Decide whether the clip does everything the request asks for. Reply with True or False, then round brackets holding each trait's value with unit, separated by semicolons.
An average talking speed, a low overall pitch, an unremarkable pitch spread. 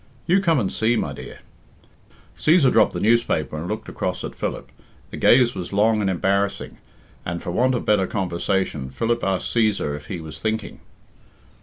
True (175 wpm; 105 Hz; 4.6 semitones)